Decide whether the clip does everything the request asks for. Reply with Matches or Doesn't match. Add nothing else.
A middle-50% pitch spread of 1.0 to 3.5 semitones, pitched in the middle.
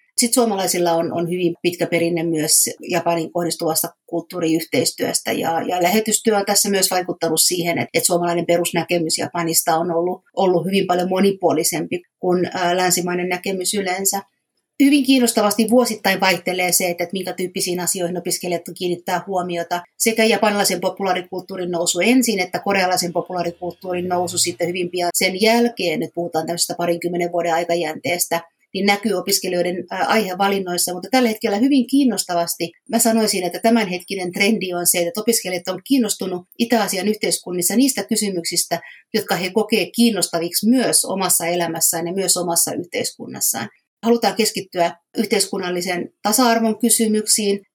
Matches